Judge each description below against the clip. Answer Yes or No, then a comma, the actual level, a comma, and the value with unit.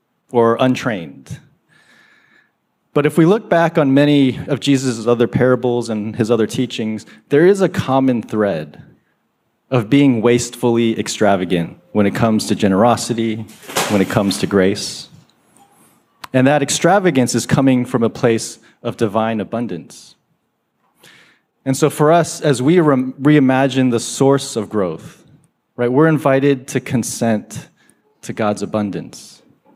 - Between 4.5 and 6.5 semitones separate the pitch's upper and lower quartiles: No, average, 3.8 semitones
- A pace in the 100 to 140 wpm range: Yes, slow, 135 wpm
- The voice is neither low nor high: No, low, 120 Hz